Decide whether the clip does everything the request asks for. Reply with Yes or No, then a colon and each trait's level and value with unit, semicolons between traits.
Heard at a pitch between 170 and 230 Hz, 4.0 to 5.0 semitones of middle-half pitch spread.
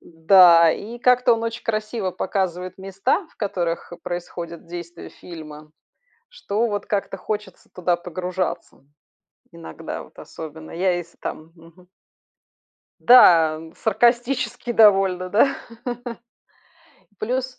Yes: medium, 185 Hz; average, 4.5 semitones